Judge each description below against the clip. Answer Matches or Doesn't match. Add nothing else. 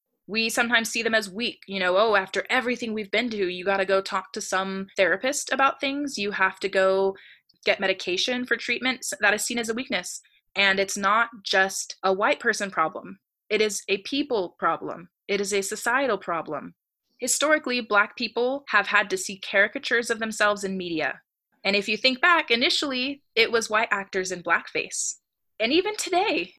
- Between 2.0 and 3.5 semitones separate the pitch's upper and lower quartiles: Doesn't match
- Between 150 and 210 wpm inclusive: Matches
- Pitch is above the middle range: Matches